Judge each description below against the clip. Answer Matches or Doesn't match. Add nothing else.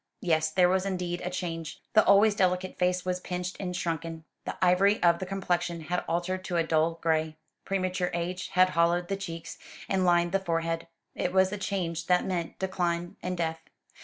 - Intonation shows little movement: Matches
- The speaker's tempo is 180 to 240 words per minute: Matches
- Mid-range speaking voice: Matches